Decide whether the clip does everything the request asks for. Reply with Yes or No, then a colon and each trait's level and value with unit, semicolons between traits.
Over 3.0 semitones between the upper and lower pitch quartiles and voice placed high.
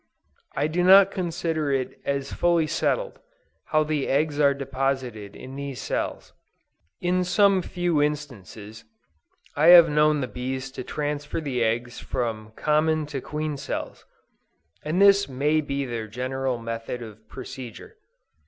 No: average, 3.7 semitones; medium, 145 Hz